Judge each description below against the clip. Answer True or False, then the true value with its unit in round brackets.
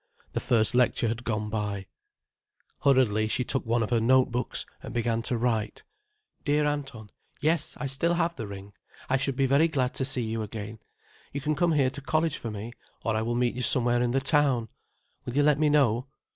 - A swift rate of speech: True (210 wpm)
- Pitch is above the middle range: False (125 Hz)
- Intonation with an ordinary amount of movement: True (3.8 semitones)